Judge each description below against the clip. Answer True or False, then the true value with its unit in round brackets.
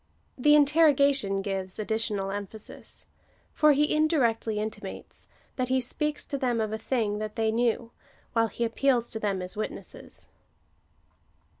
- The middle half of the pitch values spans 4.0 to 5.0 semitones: True (4.4 semitones)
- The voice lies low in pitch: False (230 Hz)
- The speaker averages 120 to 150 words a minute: True (140 wpm)